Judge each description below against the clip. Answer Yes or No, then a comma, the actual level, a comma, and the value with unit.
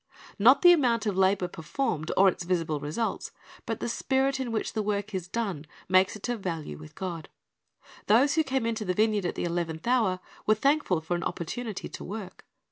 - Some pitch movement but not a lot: Yes, average, 5.0 semitones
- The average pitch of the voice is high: Yes, high, 200 Hz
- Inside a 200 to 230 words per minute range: Yes, fast, 205 wpm